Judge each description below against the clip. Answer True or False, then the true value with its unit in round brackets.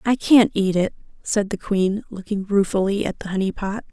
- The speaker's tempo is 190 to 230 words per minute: True (200 wpm)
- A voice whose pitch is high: True (200 Hz)